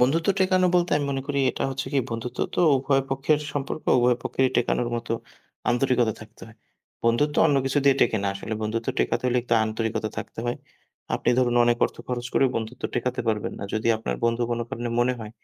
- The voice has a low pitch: Yes, low, 120 Hz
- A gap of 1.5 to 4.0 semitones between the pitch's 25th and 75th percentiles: Yes, average, 2.8 semitones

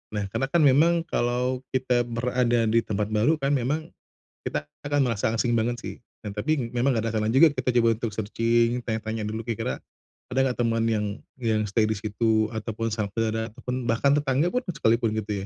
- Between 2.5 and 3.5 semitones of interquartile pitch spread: Yes, average, 2.9 semitones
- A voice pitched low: Yes, low, 115 Hz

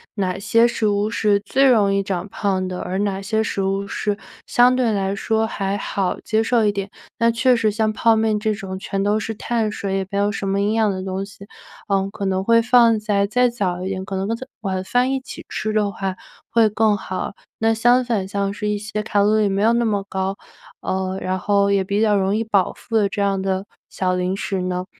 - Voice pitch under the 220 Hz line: Yes, high, 205 Hz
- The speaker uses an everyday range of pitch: No, narrow, 2.2 semitones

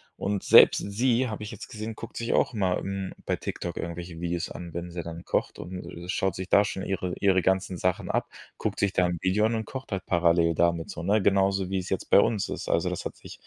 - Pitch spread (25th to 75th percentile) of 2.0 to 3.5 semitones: Yes, average, 2.7 semitones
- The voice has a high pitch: No, very low, 95 Hz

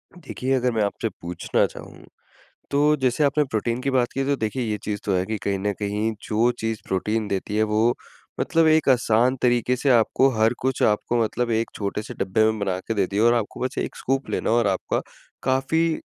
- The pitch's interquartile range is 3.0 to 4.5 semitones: Yes, average, 3.5 semitones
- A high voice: No, low, 115 Hz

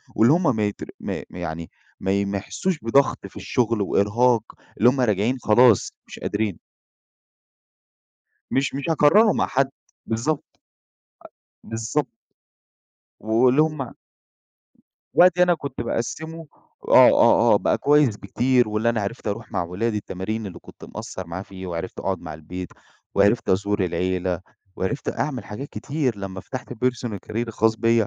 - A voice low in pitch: Yes, low, 115 Hz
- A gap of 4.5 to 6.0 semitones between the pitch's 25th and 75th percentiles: Yes, average, 4.9 semitones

